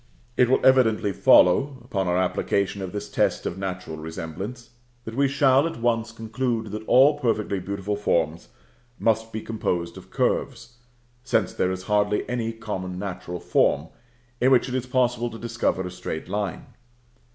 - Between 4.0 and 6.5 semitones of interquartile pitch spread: Yes, average, 4.5 semitones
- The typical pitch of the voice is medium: No, low, 105 Hz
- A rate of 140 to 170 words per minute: Yes, average, 165 wpm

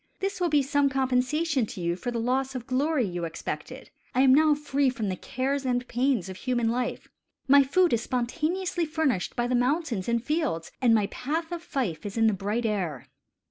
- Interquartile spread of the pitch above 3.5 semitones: Yes, average, 4.3 semitones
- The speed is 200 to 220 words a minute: Yes, fast, 205 wpm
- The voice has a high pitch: Yes, very high, 255 Hz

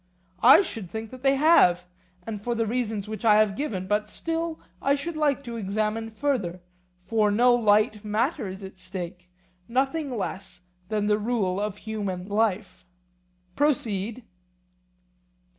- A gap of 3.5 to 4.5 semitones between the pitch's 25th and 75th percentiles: Yes, average, 3.9 semitones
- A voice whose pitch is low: No, high, 215 Hz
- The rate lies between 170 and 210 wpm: No, average, 140 wpm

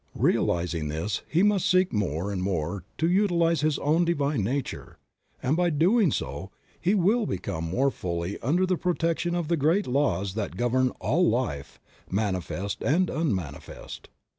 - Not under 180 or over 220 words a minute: No, average, 155 wpm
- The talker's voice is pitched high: No, medium, 140 Hz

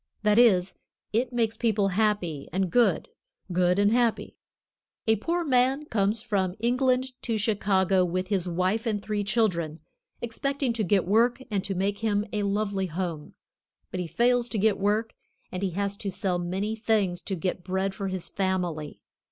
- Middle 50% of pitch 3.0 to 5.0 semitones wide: Yes, average, 3.4 semitones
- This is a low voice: No, high, 205 Hz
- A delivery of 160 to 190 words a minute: Yes, average, 170 wpm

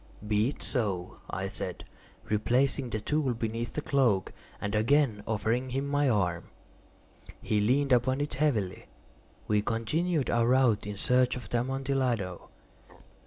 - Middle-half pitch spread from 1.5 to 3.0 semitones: No, average, 4.2 semitones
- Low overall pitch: Yes, low, 120 Hz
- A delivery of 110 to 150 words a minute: Yes, average, 140 wpm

